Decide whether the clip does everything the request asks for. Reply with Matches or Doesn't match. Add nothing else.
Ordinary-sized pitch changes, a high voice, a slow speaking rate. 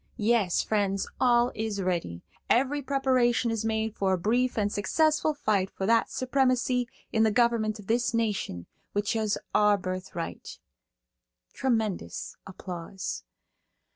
Matches